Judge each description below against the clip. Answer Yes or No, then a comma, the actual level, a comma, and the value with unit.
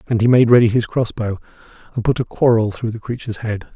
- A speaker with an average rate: No, fast, 225 wpm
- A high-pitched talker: No, low, 115 Hz